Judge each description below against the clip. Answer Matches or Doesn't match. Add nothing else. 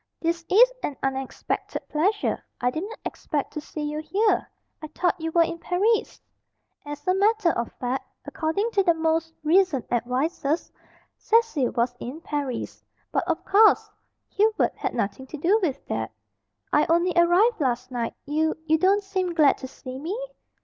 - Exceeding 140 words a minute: Matches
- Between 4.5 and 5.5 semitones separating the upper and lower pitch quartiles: Matches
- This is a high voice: Matches